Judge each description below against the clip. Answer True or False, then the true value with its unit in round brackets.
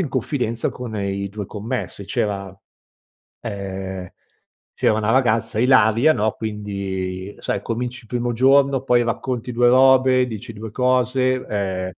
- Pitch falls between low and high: False (115 Hz)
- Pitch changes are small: False (4.0 semitones)